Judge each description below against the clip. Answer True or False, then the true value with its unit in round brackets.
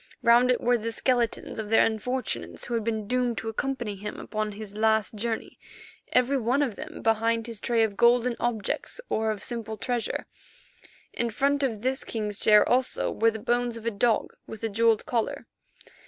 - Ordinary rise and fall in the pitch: False (2.0 semitones)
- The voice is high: True (230 Hz)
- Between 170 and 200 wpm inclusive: True (185 wpm)